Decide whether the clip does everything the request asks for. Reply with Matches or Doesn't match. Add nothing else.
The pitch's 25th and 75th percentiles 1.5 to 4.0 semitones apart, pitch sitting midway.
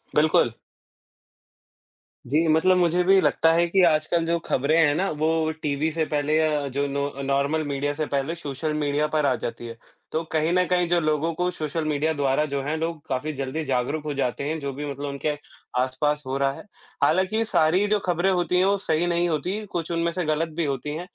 Matches